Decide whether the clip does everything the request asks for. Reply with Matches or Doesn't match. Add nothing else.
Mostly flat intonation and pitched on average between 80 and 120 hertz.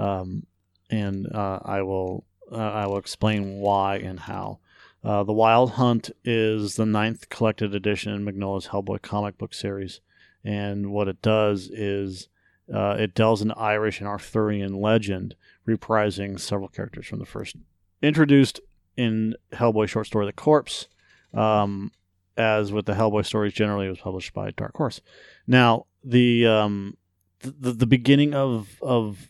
Matches